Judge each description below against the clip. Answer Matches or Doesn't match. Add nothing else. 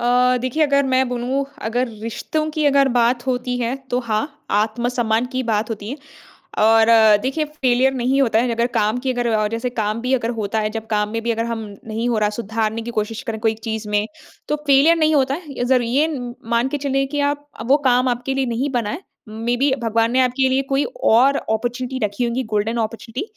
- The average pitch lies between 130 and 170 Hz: Doesn't match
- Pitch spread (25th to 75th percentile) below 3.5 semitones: Matches